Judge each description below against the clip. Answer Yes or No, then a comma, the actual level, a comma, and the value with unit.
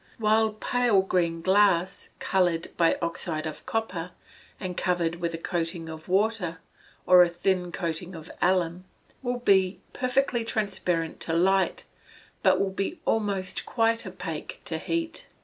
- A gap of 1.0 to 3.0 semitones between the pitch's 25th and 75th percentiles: No, average, 4.0 semitones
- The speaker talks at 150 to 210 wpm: No, average, 140 wpm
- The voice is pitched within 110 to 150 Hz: No, medium, 185 Hz